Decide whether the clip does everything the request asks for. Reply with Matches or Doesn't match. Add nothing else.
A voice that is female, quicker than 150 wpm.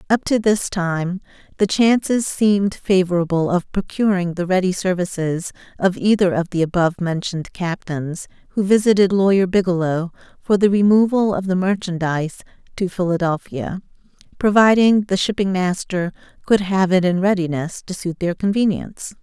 Doesn't match